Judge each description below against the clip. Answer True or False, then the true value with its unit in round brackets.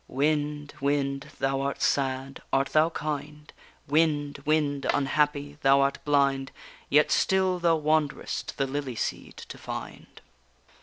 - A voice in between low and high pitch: True (145 Hz)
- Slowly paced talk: True (130 wpm)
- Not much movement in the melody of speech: True (1.7 semitones)